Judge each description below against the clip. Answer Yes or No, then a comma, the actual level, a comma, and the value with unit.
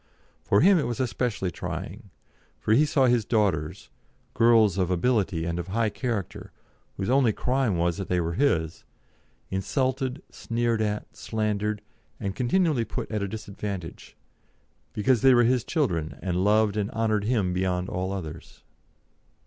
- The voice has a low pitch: Yes, low, 105 Hz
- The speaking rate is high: No, average, 150 wpm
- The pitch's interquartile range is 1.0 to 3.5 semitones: No, average, 4.6 semitones